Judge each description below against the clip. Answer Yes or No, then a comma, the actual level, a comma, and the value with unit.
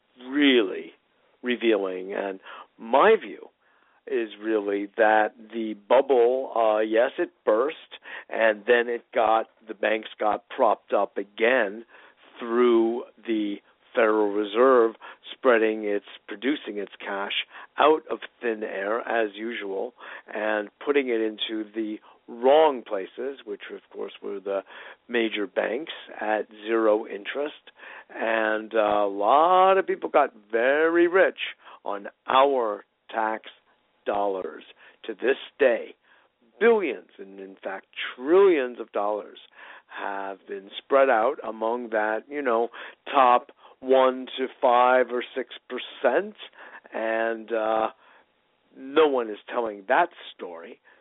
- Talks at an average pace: No, slow, 120 wpm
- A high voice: No, low, 115 Hz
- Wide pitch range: No, average, 4.3 semitones